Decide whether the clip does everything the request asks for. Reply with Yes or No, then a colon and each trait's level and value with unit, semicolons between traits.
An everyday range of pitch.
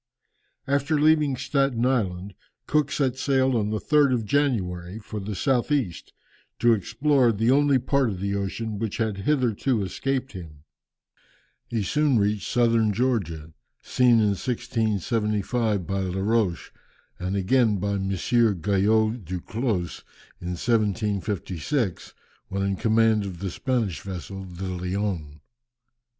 Yes: average, 4.6 semitones